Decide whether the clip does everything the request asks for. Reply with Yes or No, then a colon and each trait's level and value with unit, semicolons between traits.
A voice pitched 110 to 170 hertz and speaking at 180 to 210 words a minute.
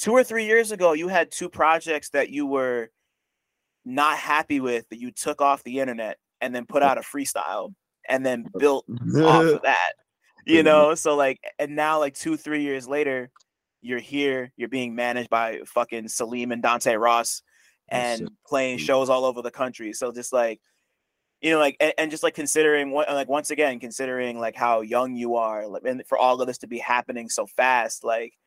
Yes: low, 135 Hz; average, 200 wpm